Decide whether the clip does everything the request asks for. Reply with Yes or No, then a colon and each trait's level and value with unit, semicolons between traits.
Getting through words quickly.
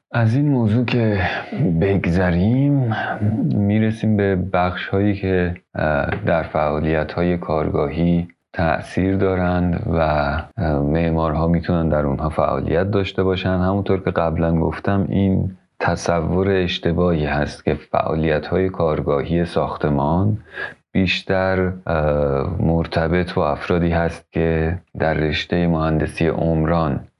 No: slow, 105 wpm